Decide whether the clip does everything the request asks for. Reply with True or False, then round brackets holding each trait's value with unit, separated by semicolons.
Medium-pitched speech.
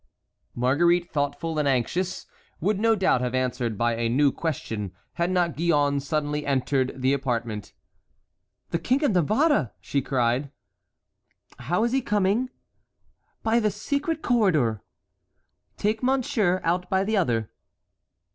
True (160 Hz)